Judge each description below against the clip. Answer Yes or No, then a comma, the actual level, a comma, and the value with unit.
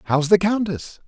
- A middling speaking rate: Yes, average, 165 wpm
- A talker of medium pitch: Yes, medium, 180 Hz